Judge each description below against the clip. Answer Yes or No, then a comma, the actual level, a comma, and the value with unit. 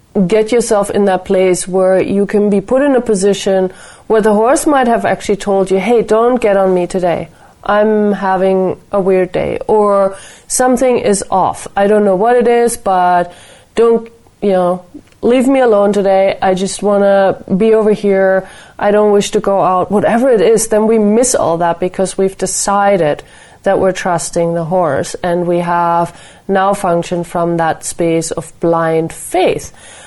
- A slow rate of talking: No, average, 180 wpm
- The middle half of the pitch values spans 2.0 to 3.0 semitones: Yes, average, 2.7 semitones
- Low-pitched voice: No, high, 195 Hz